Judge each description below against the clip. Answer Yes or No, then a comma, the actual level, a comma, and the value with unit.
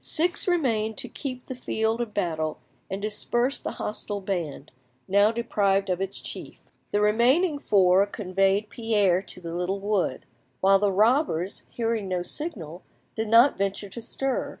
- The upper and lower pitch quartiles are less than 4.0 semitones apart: Yes, average, 3.5 semitones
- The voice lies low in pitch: No, high, 205 Hz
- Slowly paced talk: No, average, 155 wpm